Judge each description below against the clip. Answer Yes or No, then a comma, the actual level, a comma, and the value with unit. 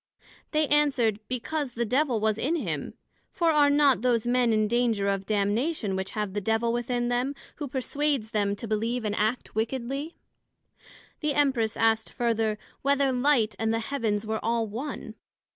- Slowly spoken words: No, average, 165 wpm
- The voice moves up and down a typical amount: Yes, average, 4.2 semitones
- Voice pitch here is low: No, high, 235 Hz